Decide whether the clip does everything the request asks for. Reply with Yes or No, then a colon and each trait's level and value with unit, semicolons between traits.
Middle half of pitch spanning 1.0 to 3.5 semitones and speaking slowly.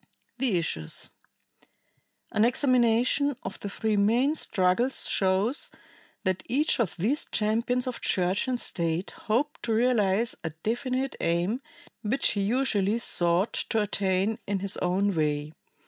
No: average, 4.7 semitones; slow, 130 wpm